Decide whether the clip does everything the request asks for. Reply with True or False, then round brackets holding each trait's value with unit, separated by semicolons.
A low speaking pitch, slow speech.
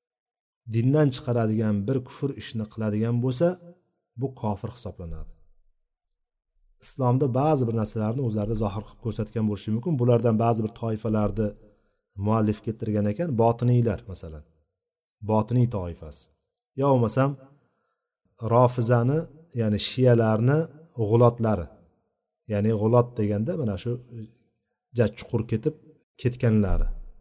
True (115 Hz; 105 wpm)